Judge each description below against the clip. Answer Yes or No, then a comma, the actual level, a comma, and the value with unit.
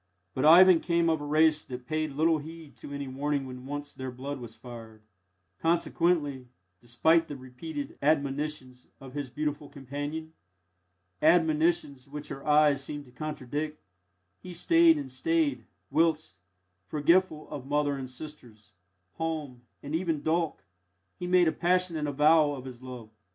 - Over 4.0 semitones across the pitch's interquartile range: No, average, 3.2 semitones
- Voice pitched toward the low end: No, medium, 150 Hz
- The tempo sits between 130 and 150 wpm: Yes, average, 145 wpm